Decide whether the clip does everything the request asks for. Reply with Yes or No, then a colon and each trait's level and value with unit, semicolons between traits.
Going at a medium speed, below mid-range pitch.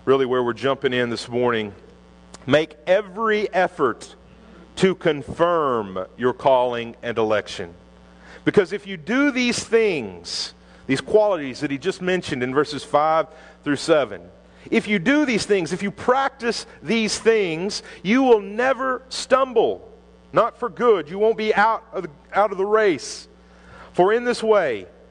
No: average, 150 wpm; medium, 185 Hz